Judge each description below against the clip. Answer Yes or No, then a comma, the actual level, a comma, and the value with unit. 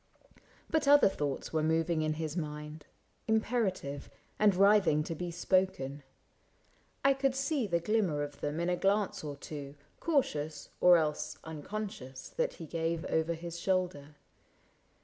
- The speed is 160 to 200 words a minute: No, average, 145 wpm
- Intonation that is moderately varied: Yes, average, 4.8 semitones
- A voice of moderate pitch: Yes, medium, 165 Hz